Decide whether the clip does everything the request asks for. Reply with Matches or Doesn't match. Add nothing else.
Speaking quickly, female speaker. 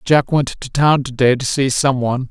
Doesn't match